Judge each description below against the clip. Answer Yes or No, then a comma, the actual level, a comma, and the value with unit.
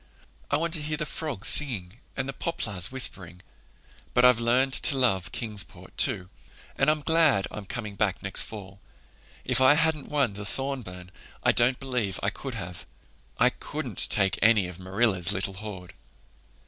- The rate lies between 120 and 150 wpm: No, average, 165 wpm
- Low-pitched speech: Yes, low, 115 Hz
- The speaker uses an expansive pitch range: Yes, wide, 5.9 semitones